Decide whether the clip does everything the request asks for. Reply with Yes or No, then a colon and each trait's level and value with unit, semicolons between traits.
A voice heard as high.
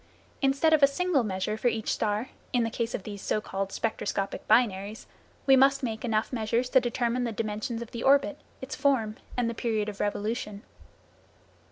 Yes: high, 230 Hz